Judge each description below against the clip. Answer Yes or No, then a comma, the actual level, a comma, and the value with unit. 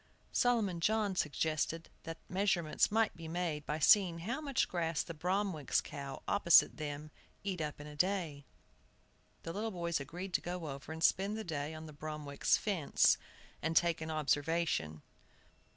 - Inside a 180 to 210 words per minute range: No, average, 160 wpm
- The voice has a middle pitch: Yes, medium, 165 Hz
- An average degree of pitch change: Yes, average, 3.7 semitones